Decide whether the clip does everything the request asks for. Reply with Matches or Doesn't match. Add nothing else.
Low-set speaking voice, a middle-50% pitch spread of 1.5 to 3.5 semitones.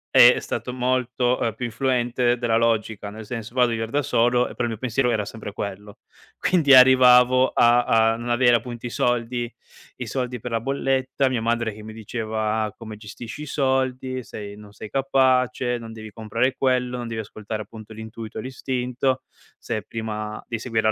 Matches